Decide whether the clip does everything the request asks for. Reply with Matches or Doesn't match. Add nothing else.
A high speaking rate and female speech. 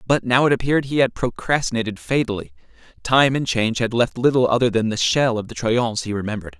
Doesn't match